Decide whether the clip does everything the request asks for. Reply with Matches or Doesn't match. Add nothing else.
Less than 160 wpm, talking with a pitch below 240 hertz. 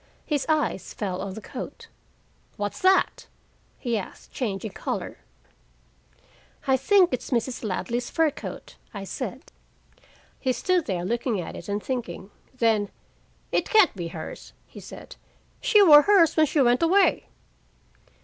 Doesn't match